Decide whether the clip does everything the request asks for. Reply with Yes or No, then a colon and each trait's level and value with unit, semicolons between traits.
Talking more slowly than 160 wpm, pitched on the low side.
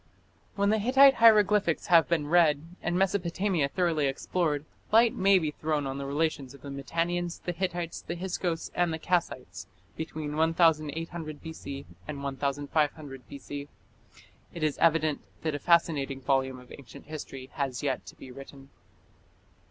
No: average, 150 wpm; medium, 155 Hz